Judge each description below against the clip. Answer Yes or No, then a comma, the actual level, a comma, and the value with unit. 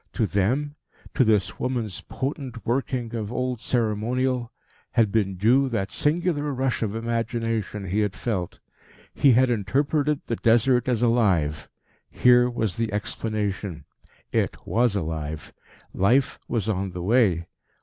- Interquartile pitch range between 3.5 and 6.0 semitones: Yes, average, 3.9 semitones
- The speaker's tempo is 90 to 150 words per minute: Yes, slow, 135 wpm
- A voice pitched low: Yes, low, 115 Hz